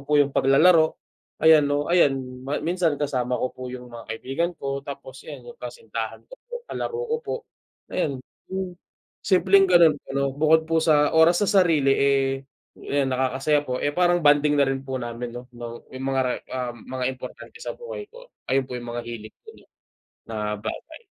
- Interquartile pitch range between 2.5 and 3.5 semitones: No, average, 4.6 semitones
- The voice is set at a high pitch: No, medium, 140 Hz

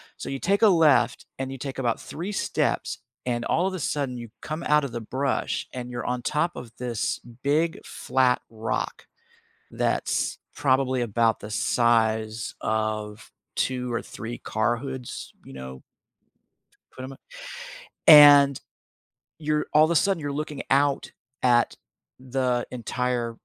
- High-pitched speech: No, low, 125 Hz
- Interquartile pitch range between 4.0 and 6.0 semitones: No, average, 3.6 semitones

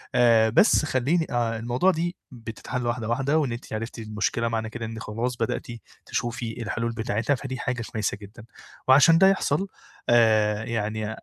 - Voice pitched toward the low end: Yes, low, 115 Hz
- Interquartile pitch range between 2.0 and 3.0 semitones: Yes, average, 2.7 semitones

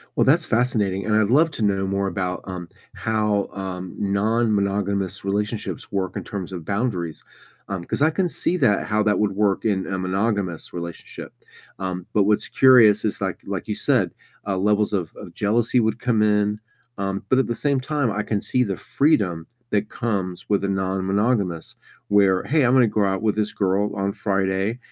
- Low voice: Yes, low, 100 Hz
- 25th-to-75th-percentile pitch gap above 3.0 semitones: No, narrow, 2.4 semitones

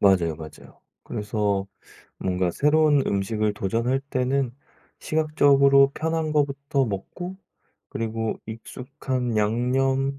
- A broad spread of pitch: No, average, 4.8 semitones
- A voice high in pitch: No, low, 125 Hz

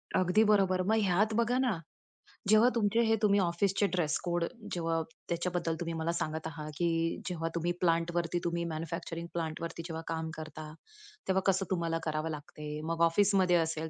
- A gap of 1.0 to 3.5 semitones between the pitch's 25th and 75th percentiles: Yes, narrow, 2.4 semitones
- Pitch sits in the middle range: Yes, medium, 170 Hz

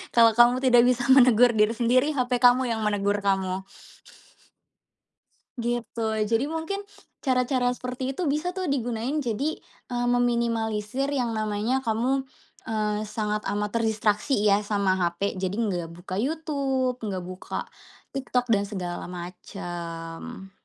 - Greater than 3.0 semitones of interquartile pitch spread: Yes, average, 3.8 semitones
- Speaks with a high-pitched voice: Yes, high, 230 Hz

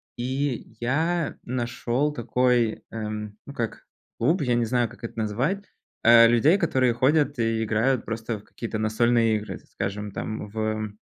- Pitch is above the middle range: No, low, 120 Hz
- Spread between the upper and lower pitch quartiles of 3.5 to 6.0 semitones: No, average, 2.8 semitones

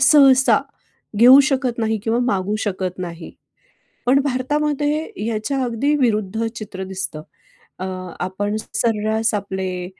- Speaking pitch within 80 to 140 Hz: No, high, 225 Hz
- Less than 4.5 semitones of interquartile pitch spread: No, wide, 5.4 semitones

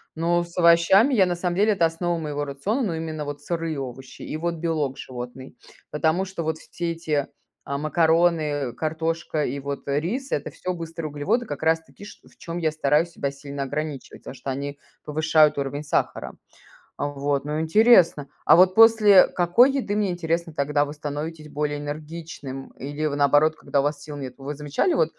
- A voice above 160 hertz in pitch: No, medium, 155 Hz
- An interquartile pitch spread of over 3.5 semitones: No, average, 2.9 semitones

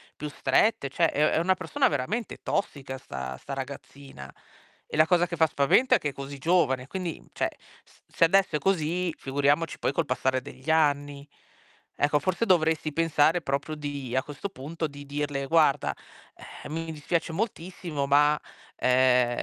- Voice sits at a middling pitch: Yes, medium, 150 Hz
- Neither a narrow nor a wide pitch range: Yes, average, 3.2 semitones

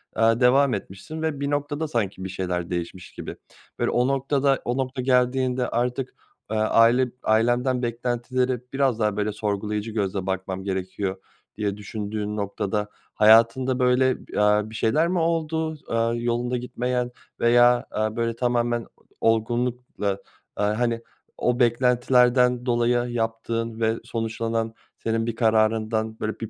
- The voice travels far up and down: No, narrow, 2.4 semitones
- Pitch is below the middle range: Yes, low, 115 Hz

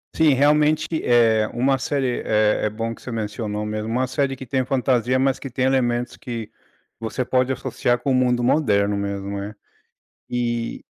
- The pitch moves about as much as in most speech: Yes, average, 3.2 semitones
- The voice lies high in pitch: No, low, 120 Hz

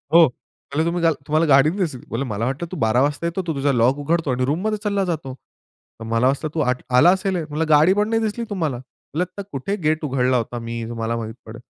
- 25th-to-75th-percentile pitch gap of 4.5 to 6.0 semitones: Yes, wide, 5.4 semitones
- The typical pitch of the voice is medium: Yes, medium, 145 Hz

